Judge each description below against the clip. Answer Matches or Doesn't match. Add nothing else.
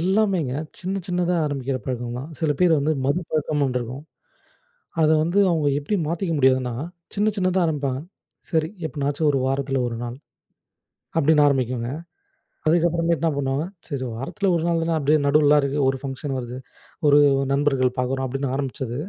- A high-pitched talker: Doesn't match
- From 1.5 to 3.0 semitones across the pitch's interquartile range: Doesn't match